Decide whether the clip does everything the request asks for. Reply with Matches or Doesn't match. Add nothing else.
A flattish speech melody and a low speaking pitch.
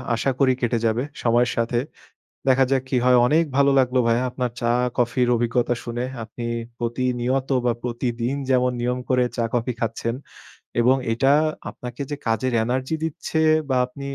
Matches